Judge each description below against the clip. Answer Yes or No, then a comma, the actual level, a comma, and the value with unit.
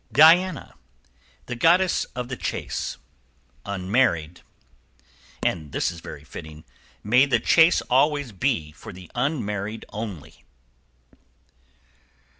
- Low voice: Yes, low, 115 Hz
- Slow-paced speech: Yes, slow, 105 wpm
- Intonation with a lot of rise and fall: Yes, wide, 8.1 semitones